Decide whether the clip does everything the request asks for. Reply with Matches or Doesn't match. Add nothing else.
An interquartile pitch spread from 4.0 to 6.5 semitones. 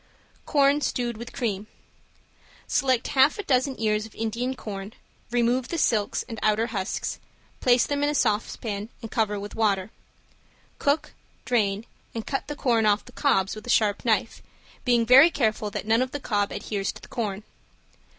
Doesn't match